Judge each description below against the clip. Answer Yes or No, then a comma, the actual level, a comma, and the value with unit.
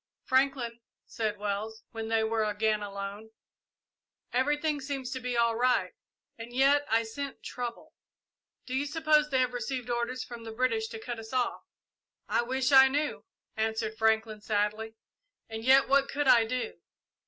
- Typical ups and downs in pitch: Yes, average, 3.1 semitones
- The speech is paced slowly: No, average, 160 wpm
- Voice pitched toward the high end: Yes, high, 235 Hz